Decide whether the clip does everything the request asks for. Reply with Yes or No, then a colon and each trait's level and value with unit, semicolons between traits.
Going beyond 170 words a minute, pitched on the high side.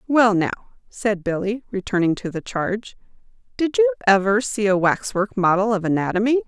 No: average, 160 wpm; high, 205 Hz